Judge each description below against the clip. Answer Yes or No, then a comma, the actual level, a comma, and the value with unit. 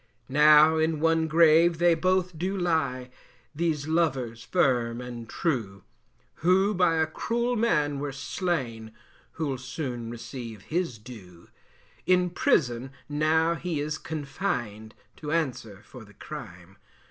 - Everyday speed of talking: No, slow, 125 wpm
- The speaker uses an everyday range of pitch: No, wide, 5.7 semitones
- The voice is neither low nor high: Yes, medium, 150 Hz